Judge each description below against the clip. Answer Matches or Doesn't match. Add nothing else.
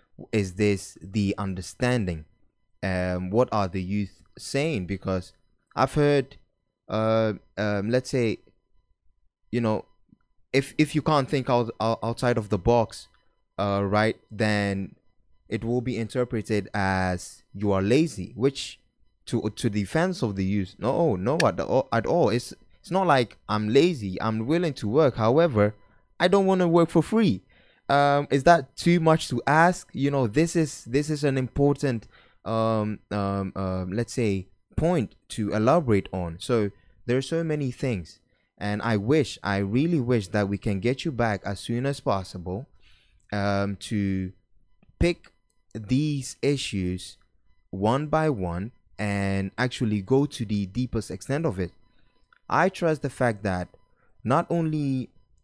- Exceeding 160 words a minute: Doesn't match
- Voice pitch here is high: Doesn't match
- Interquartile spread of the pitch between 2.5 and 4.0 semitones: Doesn't match